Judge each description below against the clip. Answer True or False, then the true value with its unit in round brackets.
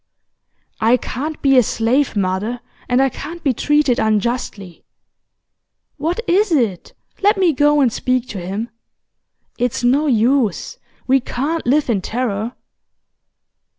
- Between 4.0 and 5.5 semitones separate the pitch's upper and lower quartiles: True (4.7 semitones)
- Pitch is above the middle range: True (250 Hz)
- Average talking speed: False (130 wpm)